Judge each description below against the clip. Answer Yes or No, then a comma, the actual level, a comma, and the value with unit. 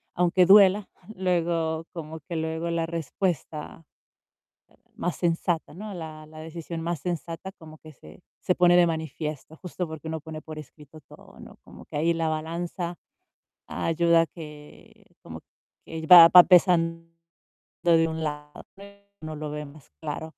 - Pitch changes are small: Yes, narrow, 1.7 semitones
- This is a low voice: No, medium, 165 Hz